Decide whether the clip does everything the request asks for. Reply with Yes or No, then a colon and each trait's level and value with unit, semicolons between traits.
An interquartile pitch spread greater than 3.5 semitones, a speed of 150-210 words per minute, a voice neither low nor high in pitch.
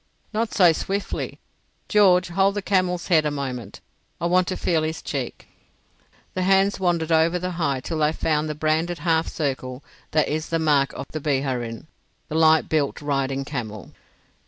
Yes: average, 4.0 semitones; average, 170 wpm; medium, 160 Hz